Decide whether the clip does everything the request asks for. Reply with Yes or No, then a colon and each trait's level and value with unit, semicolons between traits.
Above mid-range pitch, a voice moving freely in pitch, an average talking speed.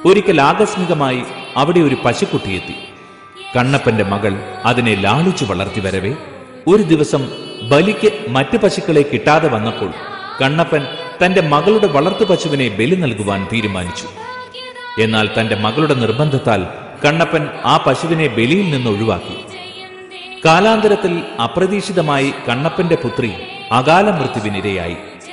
No: medium, 145 Hz; wide, 8.0 semitones; average, 100 wpm